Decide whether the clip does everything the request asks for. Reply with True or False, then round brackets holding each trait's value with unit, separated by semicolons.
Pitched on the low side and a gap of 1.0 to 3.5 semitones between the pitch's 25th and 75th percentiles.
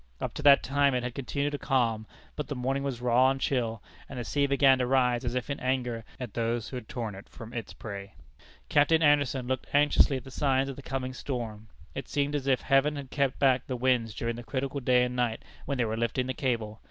True (130 Hz; 2.5 semitones)